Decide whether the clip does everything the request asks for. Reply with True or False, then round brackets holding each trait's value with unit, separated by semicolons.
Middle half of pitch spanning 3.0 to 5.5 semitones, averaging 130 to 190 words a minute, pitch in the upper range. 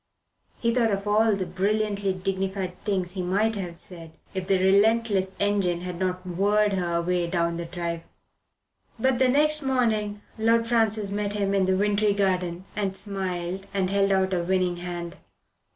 False (2.5 semitones; 170 wpm; 195 Hz)